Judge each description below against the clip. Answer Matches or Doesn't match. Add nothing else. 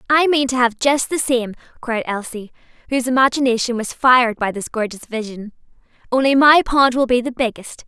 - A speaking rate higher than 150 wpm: Matches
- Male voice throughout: Doesn't match